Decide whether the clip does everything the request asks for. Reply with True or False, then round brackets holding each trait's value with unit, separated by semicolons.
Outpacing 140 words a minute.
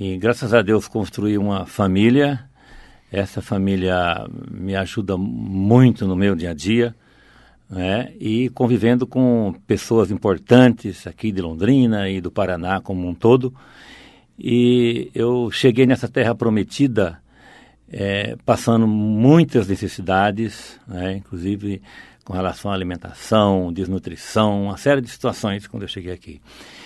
False (125 wpm)